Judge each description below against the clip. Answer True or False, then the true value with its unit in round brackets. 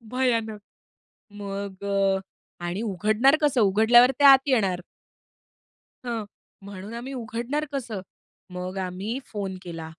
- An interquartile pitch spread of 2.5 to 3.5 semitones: False (4.0 semitones)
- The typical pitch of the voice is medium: False (215 Hz)